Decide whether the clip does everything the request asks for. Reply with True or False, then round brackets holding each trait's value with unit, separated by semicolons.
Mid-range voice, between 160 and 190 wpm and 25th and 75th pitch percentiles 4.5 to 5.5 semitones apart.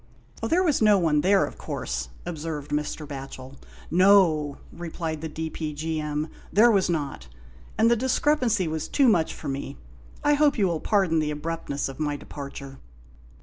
True (160 Hz; 175 wpm; 5.2 semitones)